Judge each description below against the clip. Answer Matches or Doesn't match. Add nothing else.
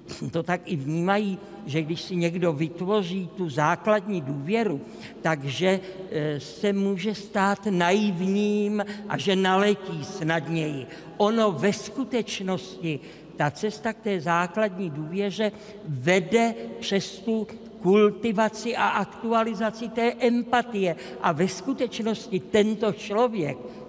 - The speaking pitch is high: Matches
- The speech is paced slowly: Matches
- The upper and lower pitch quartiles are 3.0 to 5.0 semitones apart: Matches